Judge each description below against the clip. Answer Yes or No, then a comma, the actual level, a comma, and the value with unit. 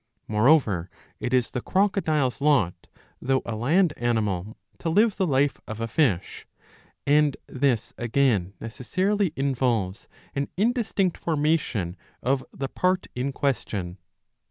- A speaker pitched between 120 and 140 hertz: Yes, low, 135 Hz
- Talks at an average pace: No, slow, 130 wpm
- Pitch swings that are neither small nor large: No, wide, 6.1 semitones